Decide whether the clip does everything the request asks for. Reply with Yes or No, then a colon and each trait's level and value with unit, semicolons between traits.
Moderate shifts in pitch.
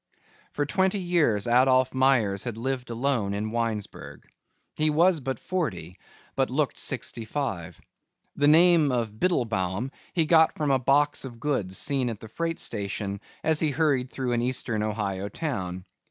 No: wide, 5.7 semitones